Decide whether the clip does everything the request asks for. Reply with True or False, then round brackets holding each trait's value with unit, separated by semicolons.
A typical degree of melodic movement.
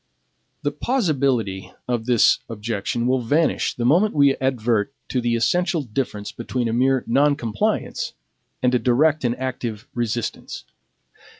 True (3.1 semitones)